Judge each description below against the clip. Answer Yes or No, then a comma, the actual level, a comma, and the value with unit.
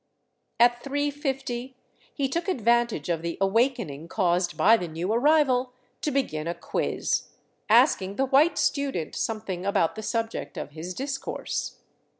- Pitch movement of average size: No, wide, 6.9 semitones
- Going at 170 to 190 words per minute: No, average, 150 wpm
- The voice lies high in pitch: Yes, high, 230 Hz